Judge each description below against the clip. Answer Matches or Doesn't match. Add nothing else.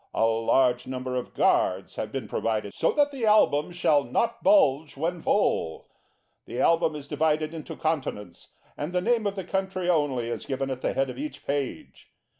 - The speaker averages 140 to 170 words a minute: Doesn't match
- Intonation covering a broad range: Matches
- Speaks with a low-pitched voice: Doesn't match